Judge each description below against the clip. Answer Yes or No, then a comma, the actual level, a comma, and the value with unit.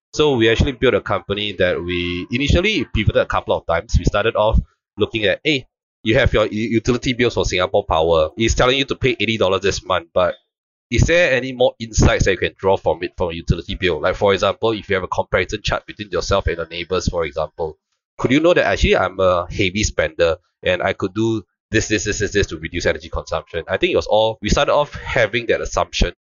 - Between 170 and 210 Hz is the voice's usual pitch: No, low, 110 Hz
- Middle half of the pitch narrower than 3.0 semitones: Yes, narrow, 2.5 semitones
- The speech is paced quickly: Yes, fast, 235 wpm